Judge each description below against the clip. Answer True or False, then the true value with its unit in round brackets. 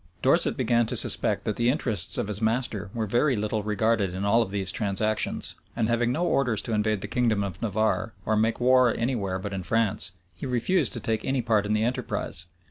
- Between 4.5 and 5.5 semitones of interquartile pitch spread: False (2.7 semitones)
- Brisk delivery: True (210 wpm)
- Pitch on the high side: False (110 Hz)